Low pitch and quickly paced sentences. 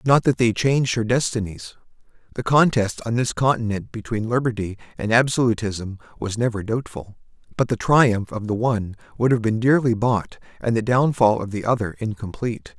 No: low, 115 Hz; average, 170 wpm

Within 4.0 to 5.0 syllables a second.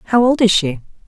No: 6.7 syllables/s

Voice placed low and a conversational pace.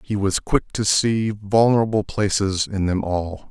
Yes: low, 100 Hz; average, 170 wpm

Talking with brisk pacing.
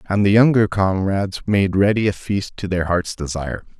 No: average, 190 wpm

